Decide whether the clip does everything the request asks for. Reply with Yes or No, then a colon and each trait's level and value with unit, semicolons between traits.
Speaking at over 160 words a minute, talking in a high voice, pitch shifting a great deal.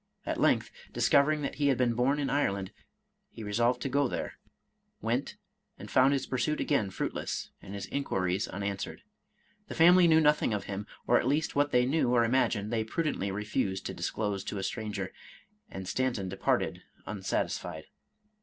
No: average, 175 wpm; low, 120 Hz; wide, 6.0 semitones